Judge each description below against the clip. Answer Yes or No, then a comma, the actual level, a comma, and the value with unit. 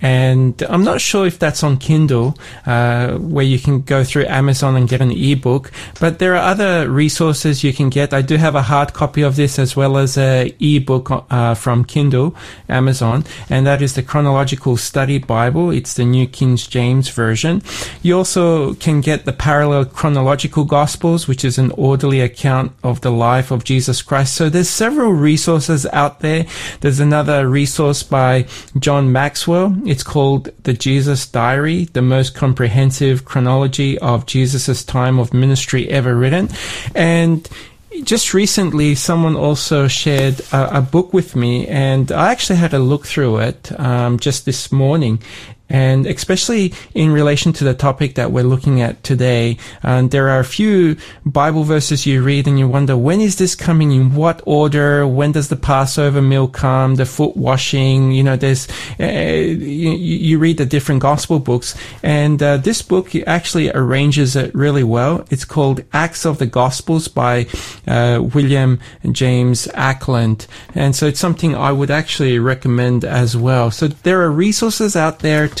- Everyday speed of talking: Yes, average, 170 wpm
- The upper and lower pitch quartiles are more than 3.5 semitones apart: No, average, 3.1 semitones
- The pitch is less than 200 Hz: Yes, medium, 140 Hz